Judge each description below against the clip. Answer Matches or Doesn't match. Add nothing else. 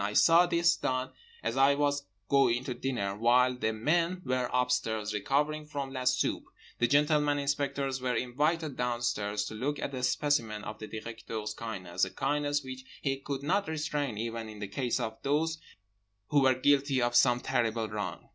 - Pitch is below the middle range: Matches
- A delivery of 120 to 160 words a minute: Doesn't match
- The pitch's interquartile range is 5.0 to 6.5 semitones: Doesn't match